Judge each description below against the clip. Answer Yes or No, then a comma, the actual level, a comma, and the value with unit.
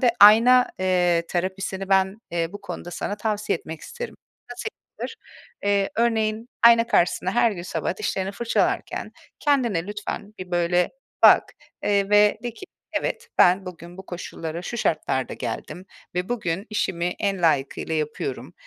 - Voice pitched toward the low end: No, high, 195 Hz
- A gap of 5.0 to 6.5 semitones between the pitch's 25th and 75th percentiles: No, average, 3.6 semitones